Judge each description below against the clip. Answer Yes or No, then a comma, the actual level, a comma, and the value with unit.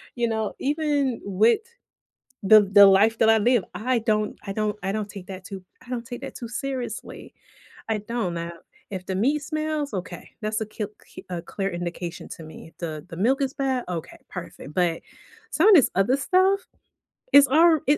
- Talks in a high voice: Yes, high, 220 Hz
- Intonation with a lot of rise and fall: Yes, wide, 6.0 semitones